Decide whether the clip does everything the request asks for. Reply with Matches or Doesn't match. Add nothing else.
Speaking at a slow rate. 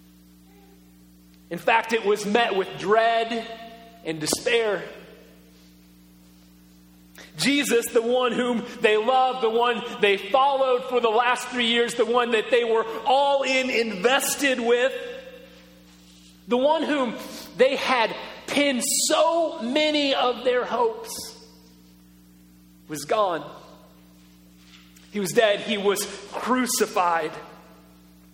Matches